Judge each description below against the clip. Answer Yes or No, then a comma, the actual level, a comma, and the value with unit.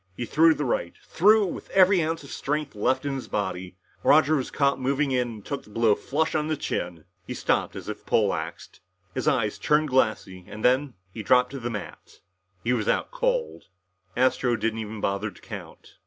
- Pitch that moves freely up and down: Yes, wide, 5.7 semitones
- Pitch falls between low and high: No, low, 130 Hz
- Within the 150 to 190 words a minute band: No, average, 200 wpm